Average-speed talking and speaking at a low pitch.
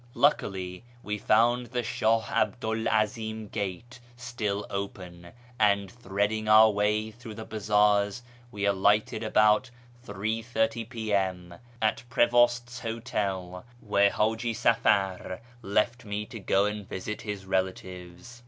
No: slow, 120 wpm; low, 105 Hz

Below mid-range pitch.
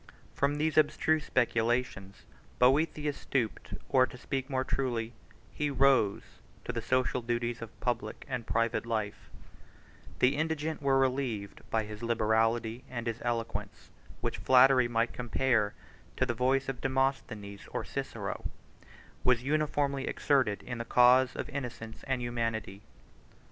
Yes: low, 125 Hz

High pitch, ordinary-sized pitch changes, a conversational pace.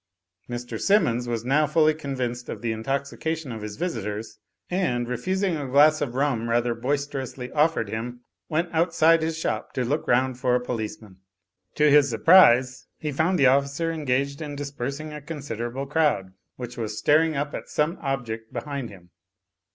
No: low, 135 Hz; average, 4.1 semitones; average, 165 wpm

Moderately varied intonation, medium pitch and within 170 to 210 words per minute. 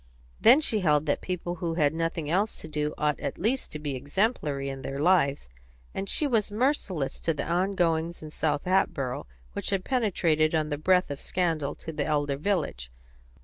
Yes: average, 4.2 semitones; medium, 160 Hz; average, 190 wpm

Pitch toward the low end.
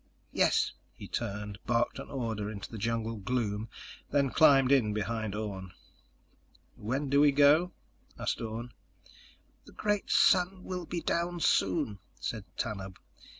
Yes: low, 115 Hz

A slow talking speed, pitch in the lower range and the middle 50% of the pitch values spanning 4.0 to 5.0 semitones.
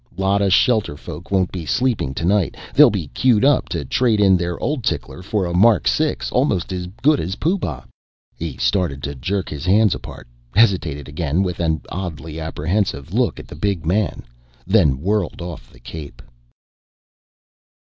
No: average, 165 wpm; very low, 90 Hz; average, 4.4 semitones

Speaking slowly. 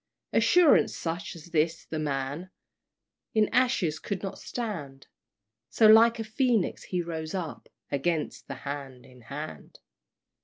Yes: slow, 130 wpm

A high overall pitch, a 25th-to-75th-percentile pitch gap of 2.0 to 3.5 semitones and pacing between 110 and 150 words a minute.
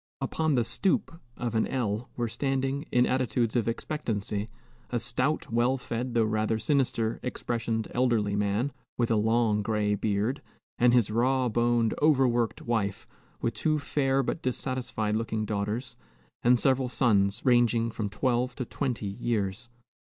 No: low, 120 Hz; average, 2.9 semitones; average, 145 wpm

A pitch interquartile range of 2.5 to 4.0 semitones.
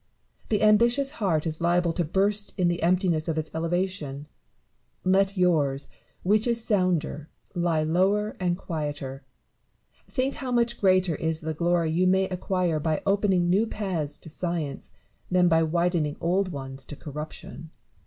Yes: average, 3.5 semitones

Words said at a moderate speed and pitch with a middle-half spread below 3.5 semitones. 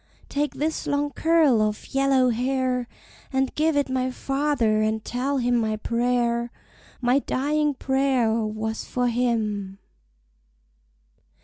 No: slow, 120 wpm; average, 3.1 semitones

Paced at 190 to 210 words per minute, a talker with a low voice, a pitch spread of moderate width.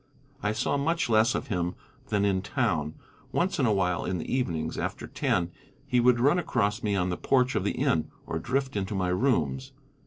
No: fast, 205 wpm; low, 105 Hz; wide, 6.0 semitones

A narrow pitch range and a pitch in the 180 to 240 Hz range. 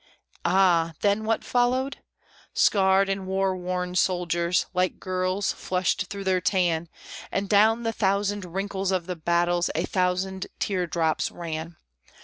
Yes: narrow, 2.1 semitones; medium, 185 Hz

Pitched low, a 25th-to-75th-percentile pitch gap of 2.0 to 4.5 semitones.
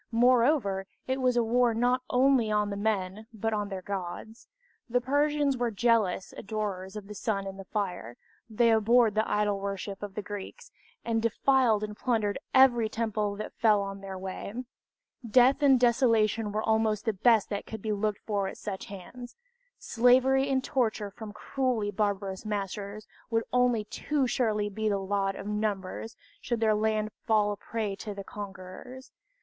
No: high, 215 Hz; average, 2.9 semitones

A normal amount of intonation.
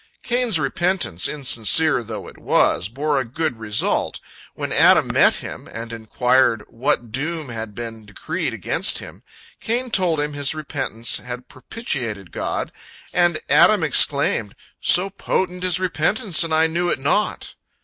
No: wide, 7.0 semitones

